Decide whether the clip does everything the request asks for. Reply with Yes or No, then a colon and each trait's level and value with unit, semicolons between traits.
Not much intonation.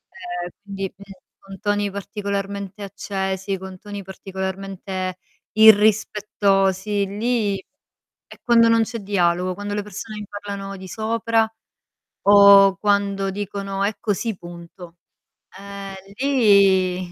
Yes: narrow, 1.4 semitones